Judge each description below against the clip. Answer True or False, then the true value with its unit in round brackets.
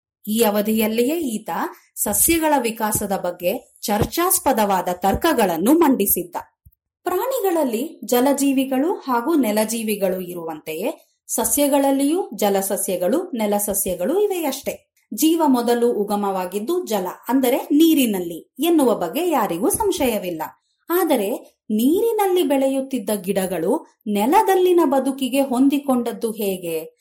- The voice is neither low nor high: False (255 Hz)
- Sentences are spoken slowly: False (80 wpm)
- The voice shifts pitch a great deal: True (6.8 semitones)